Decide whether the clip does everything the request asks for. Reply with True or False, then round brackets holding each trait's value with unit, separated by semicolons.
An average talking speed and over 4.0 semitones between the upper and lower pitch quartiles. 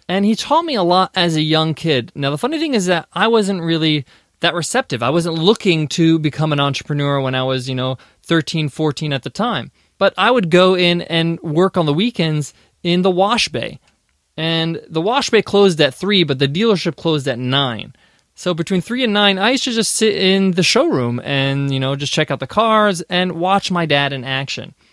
False (220 wpm; 5.4 semitones)